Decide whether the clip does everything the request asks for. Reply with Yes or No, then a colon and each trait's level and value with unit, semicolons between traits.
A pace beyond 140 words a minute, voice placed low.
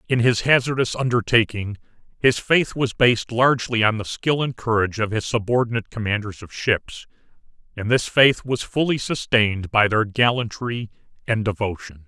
Yes: average, 155 wpm; low, 115 Hz